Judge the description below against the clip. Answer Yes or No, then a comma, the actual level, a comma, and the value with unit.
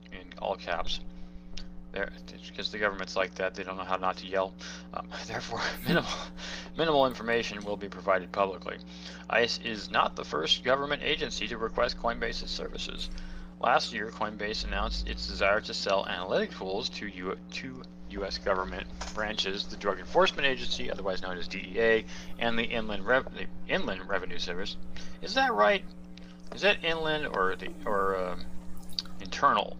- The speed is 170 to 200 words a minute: No, average, 155 wpm